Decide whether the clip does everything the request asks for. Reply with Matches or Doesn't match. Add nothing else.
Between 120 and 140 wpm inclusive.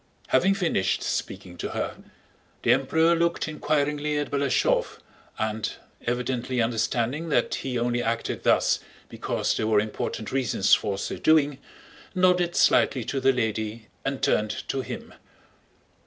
Matches